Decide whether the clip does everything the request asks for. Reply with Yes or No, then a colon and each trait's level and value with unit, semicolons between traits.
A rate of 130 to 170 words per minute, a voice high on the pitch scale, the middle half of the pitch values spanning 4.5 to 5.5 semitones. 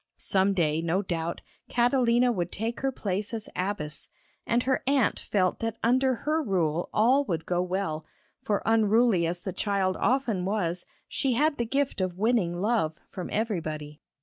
Yes: average, 165 wpm; high, 200 Hz; average, 5.2 semitones